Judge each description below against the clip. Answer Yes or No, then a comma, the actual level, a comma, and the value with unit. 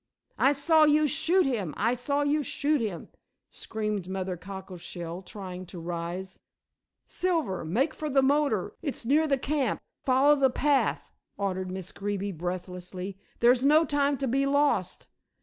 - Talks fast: No, average, 150 wpm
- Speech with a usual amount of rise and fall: No, wide, 7.5 semitones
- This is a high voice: Yes, high, 235 Hz